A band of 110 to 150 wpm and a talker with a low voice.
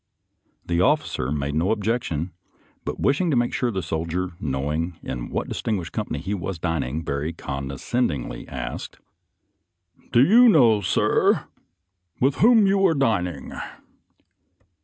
Yes: average, 145 wpm; very low, 90 Hz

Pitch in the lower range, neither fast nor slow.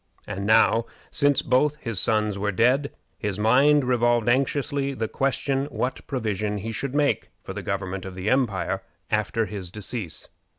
Yes: low, 115 Hz; average, 160 wpm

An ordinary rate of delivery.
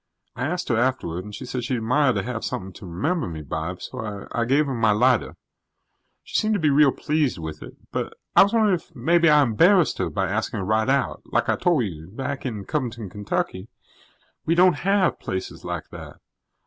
No: fast, 210 wpm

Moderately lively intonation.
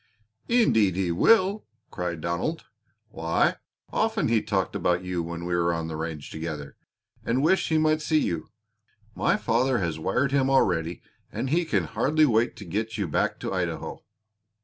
No: wide, 8.4 semitones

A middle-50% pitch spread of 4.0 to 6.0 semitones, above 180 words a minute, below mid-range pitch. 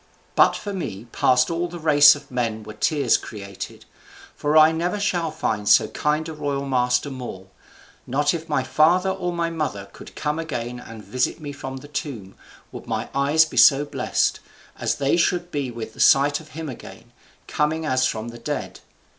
No: average, 4.4 semitones; average, 190 wpm; medium, 145 Hz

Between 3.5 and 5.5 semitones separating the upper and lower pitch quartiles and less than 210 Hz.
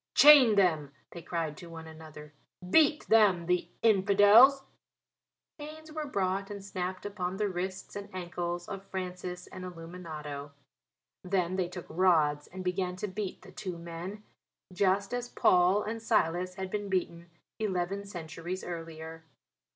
No: average, 2.8 semitones; medium, 185 Hz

